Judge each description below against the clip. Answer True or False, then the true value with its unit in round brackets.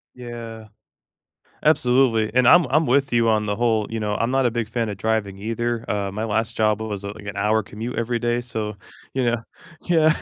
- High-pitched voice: False (115 Hz)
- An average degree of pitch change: False (2.3 semitones)